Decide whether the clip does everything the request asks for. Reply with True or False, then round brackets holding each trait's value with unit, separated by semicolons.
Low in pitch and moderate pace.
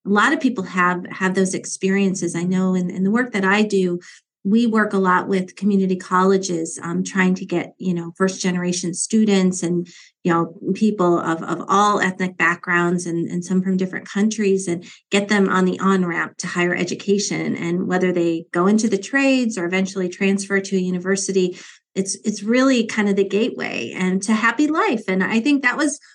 False (190 Hz; 195 wpm)